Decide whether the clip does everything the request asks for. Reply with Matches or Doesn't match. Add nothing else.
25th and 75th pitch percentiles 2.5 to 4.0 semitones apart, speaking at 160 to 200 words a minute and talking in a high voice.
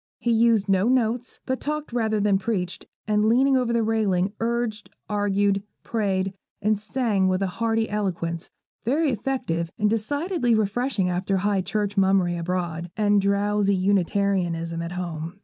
Doesn't match